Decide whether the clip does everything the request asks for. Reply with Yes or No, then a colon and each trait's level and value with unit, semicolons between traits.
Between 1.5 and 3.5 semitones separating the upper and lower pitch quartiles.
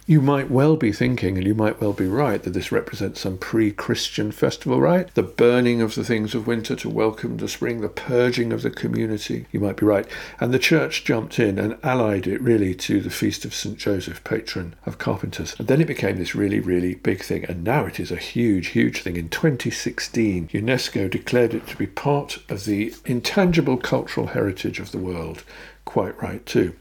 No: average, 4.2 semitones